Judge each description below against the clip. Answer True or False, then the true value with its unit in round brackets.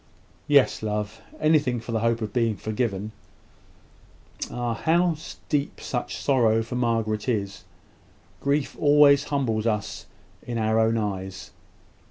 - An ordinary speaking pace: False (125 wpm)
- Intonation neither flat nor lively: True (4.1 semitones)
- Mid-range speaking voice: False (115 Hz)